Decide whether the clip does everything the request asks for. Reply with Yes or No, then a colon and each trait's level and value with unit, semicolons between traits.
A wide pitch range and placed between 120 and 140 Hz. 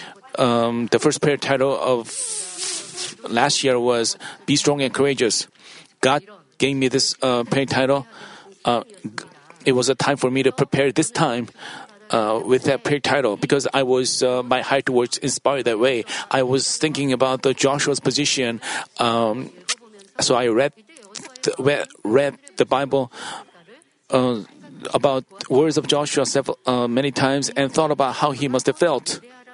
No: narrow, 1.8 semitones; low, 135 Hz